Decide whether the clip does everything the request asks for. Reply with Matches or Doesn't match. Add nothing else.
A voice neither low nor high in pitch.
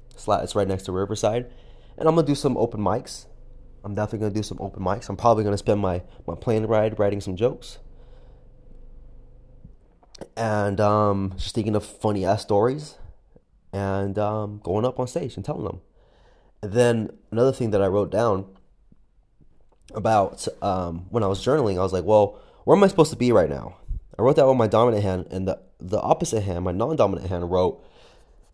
Doesn't match